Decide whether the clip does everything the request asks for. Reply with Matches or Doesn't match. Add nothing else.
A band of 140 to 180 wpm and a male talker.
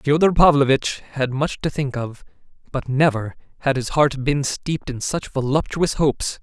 Matches